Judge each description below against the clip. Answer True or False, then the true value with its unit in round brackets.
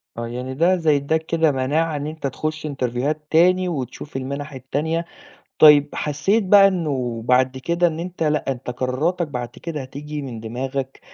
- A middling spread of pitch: True (3.9 semitones)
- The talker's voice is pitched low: False (145 Hz)